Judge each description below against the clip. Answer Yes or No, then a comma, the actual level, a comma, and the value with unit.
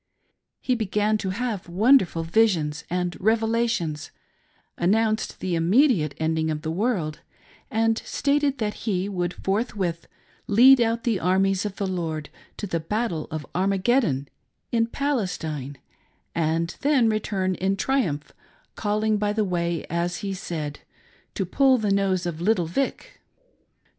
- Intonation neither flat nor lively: Yes, average, 4.9 semitones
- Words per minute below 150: Yes, average, 140 wpm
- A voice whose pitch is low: No, high, 195 Hz